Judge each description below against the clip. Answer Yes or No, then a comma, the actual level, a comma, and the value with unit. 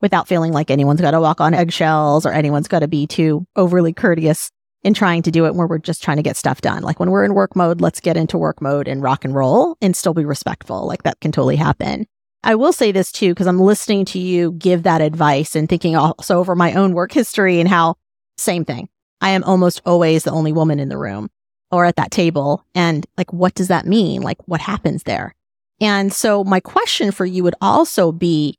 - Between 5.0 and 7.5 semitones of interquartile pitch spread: No, average, 3.4 semitones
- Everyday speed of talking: No, fast, 235 wpm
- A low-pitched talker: No, medium, 175 Hz